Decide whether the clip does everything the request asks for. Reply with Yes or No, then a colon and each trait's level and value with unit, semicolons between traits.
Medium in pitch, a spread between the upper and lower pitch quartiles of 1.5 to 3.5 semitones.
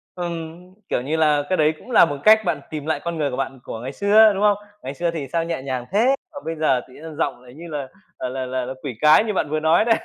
No: medium, 155 Hz; average, 4.4 semitones